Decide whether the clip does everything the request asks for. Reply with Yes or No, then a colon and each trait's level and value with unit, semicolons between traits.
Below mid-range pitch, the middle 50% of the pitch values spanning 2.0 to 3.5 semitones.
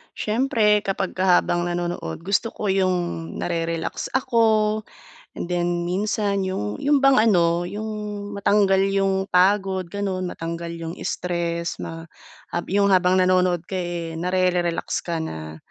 No: medium, 185 Hz; average, 2.7 semitones